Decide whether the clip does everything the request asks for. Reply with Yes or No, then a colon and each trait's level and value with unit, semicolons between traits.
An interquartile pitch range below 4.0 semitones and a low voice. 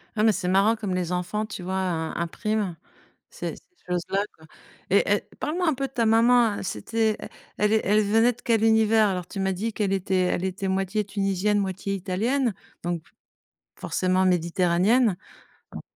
No: average, 3.3 semitones; high, 195 Hz